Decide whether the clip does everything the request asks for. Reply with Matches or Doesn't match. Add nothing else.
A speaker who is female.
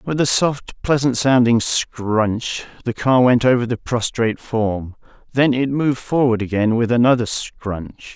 Doesn't match